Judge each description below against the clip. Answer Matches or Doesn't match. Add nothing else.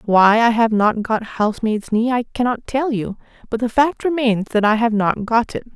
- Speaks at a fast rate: Matches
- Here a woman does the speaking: Matches